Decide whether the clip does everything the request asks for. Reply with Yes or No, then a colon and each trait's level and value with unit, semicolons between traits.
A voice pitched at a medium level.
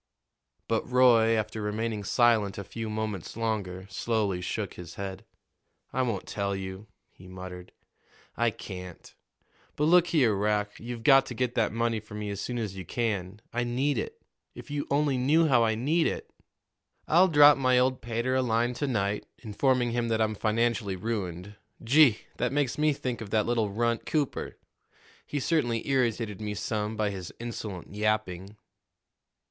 No: low, 115 Hz